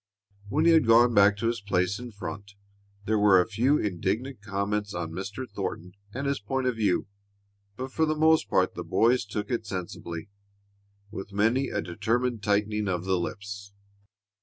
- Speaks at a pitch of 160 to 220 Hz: No, low, 105 Hz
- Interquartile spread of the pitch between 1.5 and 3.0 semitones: No, average, 3.6 semitones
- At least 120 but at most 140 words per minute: No, average, 175 wpm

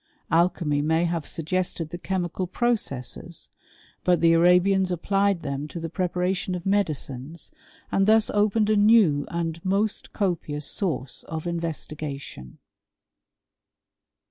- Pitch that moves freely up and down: No, average, 3.7 semitones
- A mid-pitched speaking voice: Yes, medium, 175 Hz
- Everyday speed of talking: No, slow, 125 wpm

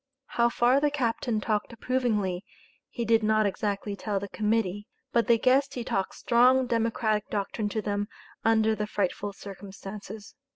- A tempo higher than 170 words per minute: No, average, 155 wpm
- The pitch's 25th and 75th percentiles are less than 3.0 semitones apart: Yes, narrow, 2.5 semitones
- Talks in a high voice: Yes, high, 215 Hz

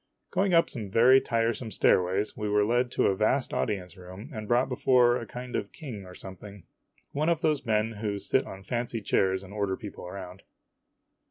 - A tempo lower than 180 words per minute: No, average, 190 wpm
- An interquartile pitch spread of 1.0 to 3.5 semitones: No, average, 4.1 semitones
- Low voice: Yes, low, 110 Hz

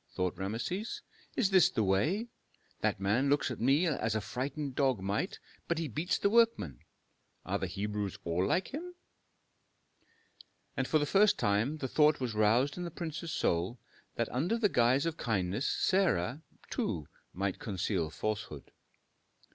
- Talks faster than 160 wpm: No, average, 155 wpm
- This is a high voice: No, low, 125 Hz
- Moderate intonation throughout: No, wide, 8.2 semitones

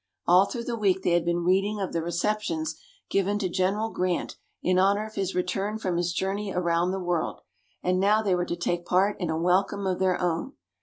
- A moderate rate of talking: No, fast, 215 wpm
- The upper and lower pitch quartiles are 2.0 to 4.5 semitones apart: Yes, narrow, 2.4 semitones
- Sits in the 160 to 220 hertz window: Yes, medium, 185 Hz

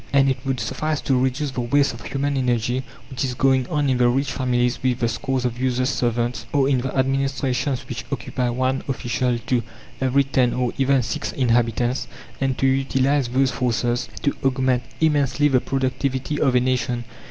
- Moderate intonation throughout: No, narrow, 1.7 semitones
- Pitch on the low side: Yes, low, 130 Hz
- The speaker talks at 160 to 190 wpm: Yes, average, 185 wpm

